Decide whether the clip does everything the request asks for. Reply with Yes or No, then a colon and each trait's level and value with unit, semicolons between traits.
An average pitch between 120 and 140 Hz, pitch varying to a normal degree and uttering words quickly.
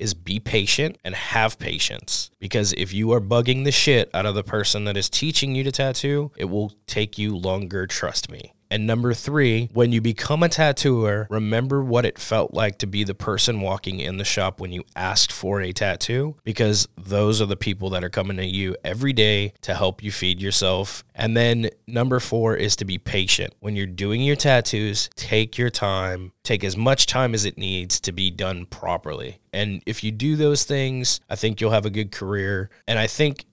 No: low, 105 Hz; average, 3.5 semitones; fast, 210 wpm